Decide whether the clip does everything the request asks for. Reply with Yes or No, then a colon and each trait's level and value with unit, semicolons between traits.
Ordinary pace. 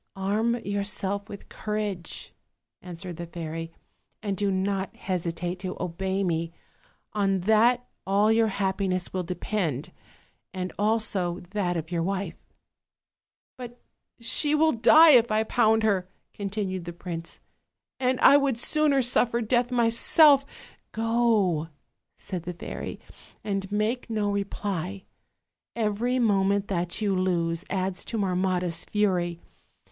No: slow, 130 wpm